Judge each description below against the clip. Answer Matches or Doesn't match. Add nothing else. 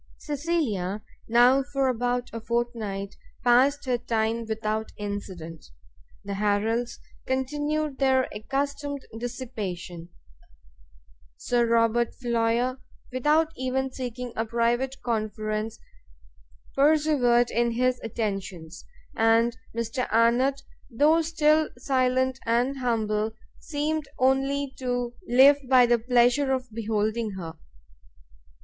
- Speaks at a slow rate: Matches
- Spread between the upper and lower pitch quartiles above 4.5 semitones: Doesn't match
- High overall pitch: Matches